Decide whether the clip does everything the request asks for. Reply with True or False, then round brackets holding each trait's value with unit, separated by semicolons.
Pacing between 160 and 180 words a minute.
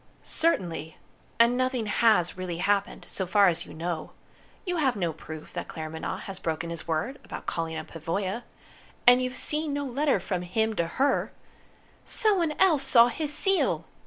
True (170 wpm)